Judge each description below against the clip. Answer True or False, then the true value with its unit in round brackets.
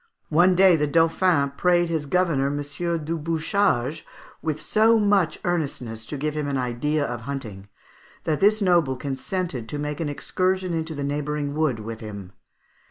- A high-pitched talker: False (150 Hz)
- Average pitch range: True (4.0 semitones)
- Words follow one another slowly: False (165 wpm)